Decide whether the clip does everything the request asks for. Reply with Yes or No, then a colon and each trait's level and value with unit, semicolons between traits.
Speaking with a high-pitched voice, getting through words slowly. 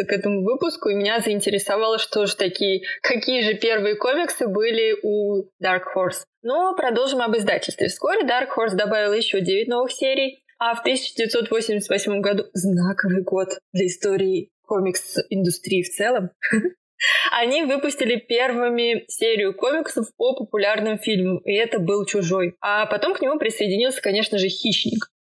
No: high, 215 Hz; average, 145 wpm